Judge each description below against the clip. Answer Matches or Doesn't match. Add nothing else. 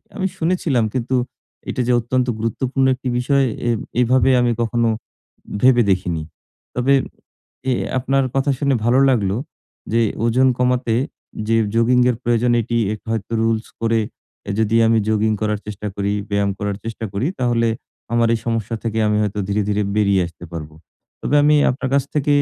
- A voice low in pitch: Matches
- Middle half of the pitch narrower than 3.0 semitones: Doesn't match